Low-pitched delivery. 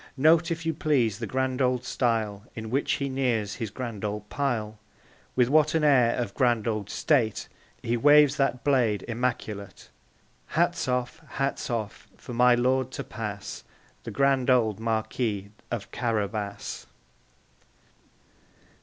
Yes: low, 120 Hz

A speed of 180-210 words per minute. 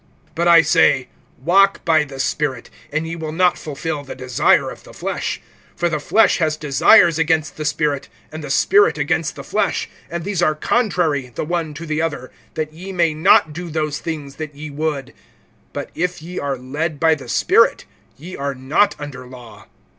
Yes: average, 190 wpm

